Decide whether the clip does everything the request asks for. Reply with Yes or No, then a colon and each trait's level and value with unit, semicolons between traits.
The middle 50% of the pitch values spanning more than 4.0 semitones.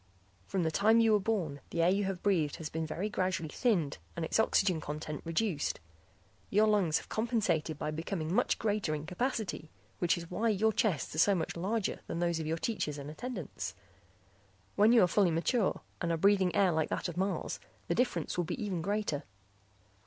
Yes: average, 4.6 semitones